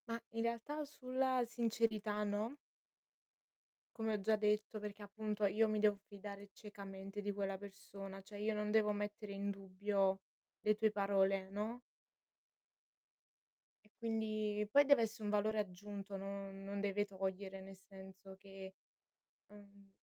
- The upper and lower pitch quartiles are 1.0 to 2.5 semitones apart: Yes, narrow, 1.6 semitones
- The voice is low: No, high, 205 Hz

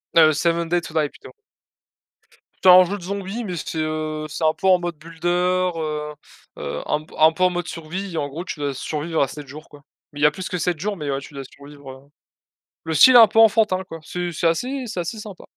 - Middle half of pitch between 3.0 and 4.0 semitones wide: Yes, average, 3.3 semitones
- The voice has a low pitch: No, medium, 165 Hz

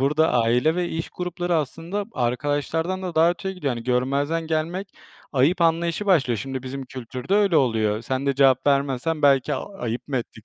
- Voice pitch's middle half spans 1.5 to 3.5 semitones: No, average, 4.7 semitones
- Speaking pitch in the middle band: Yes, medium, 145 Hz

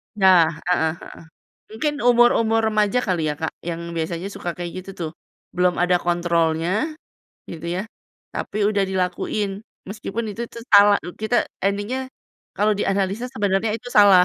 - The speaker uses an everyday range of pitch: Yes, average, 3.5 semitones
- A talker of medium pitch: No, high, 195 Hz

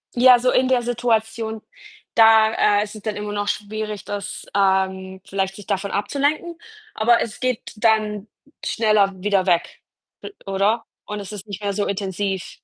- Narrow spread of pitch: Yes, narrow, 2.1 semitones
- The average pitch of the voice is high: Yes, high, 210 Hz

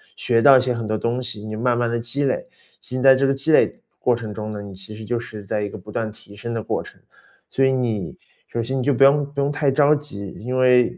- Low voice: Yes, low, 120 Hz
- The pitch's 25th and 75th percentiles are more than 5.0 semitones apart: No, average, 3.7 semitones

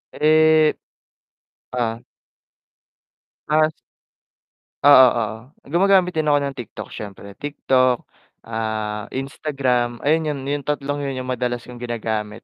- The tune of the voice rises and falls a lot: No, average, 4.0 semitones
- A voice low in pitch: Yes, low, 130 Hz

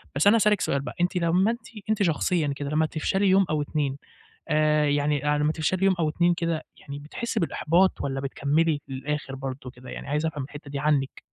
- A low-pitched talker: No, medium, 150 Hz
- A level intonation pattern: No, average, 3.4 semitones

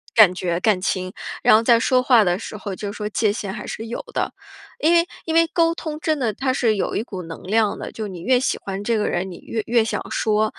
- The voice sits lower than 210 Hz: No, high, 215 Hz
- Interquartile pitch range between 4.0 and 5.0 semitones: Yes, average, 4.4 semitones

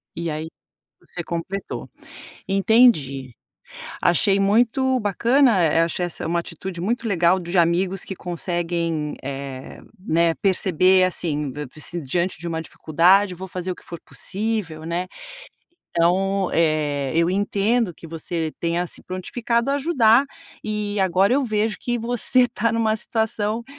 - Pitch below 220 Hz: Yes, medium, 185 Hz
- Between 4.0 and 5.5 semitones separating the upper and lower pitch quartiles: Yes, average, 4.3 semitones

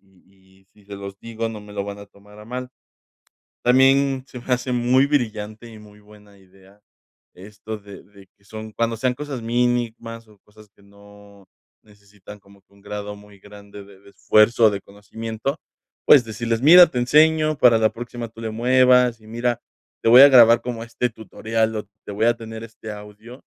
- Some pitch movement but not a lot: Yes, average, 3.0 semitones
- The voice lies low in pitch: Yes, low, 110 Hz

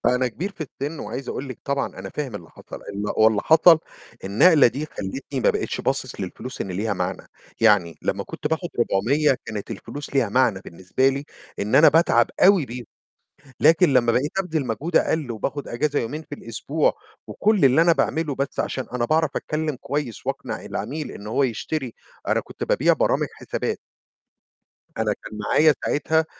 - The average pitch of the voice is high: No, low, 135 Hz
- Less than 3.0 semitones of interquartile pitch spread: No, wide, 5.4 semitones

